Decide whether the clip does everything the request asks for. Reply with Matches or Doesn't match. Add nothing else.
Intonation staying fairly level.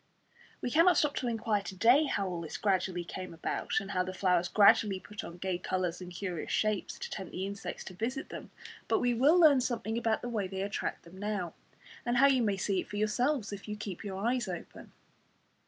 Doesn't match